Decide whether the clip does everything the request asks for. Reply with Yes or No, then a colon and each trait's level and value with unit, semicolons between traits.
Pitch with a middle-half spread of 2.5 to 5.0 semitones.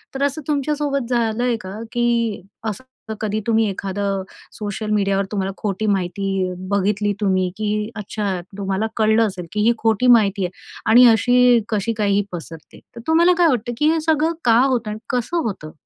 Yes: average, 3.7 semitones